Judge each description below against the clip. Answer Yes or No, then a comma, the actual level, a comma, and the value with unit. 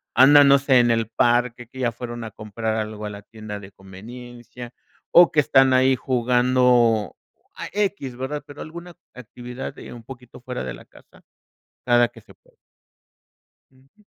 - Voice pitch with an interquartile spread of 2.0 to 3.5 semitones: Yes, narrow, 2.5 semitones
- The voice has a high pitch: No, low, 120 Hz